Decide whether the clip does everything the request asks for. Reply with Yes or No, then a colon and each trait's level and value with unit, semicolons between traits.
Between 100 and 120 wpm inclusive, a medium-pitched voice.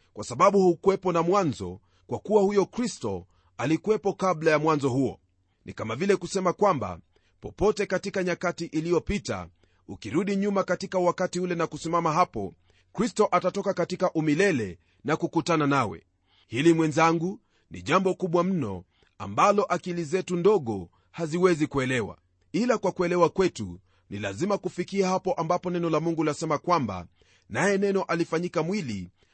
No: fast, 140 wpm; medium, 165 Hz